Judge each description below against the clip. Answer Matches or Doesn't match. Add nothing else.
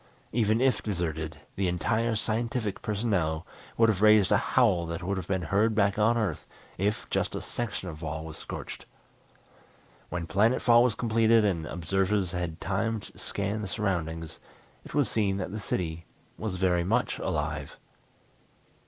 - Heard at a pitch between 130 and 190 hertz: Doesn't match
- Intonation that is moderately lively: Matches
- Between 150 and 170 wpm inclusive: Matches